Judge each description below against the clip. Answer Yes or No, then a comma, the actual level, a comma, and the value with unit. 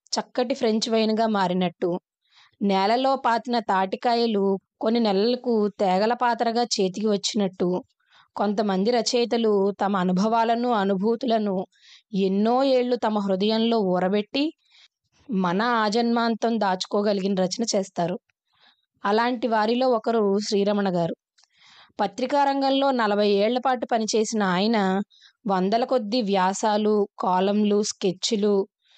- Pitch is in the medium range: No, high, 215 Hz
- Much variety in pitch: No, average, 3.2 semitones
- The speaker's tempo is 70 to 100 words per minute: Yes, average, 95 wpm